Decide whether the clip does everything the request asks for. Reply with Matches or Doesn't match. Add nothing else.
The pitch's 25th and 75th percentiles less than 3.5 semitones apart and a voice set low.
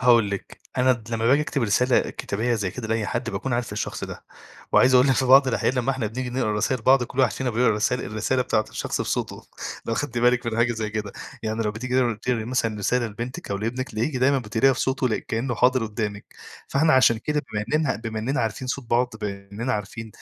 Matches